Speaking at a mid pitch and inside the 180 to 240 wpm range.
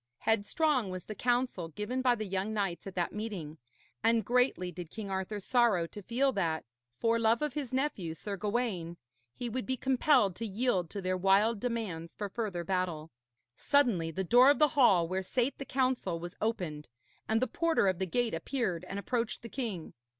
No: high, 210 Hz; average, 190 wpm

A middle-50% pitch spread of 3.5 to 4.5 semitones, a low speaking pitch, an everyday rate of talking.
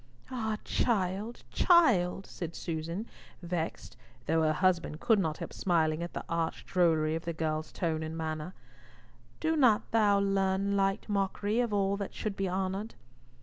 No: average, 3.9 semitones; high, 190 Hz; average, 155 wpm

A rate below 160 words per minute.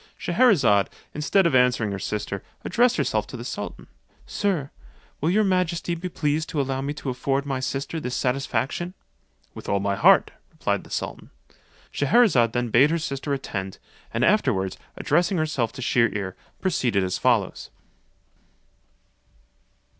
Yes: average, 145 wpm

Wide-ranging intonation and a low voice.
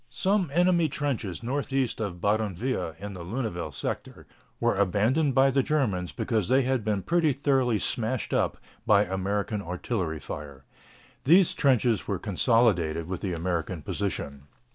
Yes: wide, 6.5 semitones; low, 110 Hz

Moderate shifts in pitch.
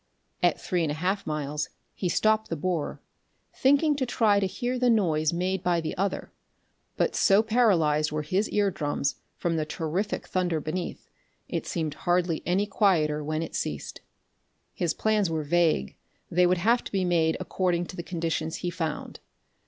Yes: average, 3.9 semitones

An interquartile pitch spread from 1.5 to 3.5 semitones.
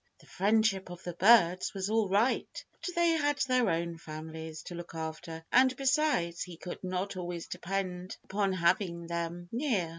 No: average, 4.6 semitones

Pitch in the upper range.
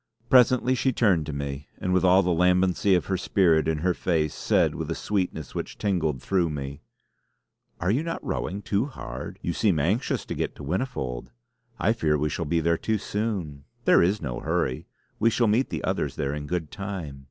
No: very low, 90 Hz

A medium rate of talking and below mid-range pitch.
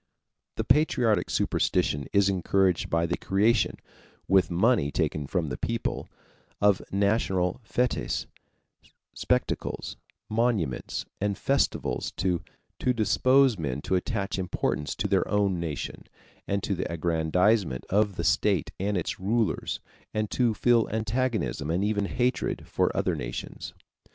No: slow, 125 wpm; low, 100 Hz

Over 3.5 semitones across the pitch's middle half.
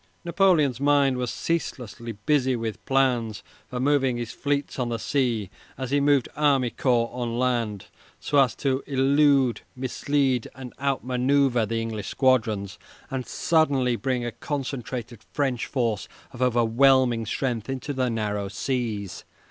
No: average, 2.9 semitones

